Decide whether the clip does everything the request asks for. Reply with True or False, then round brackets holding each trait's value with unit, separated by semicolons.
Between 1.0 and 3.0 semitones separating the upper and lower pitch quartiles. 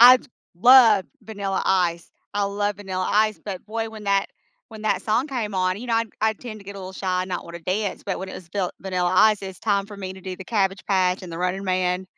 True (2.5 semitones)